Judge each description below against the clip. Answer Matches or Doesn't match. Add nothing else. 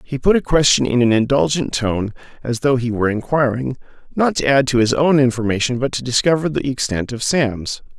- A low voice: Matches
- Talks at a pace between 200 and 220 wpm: Matches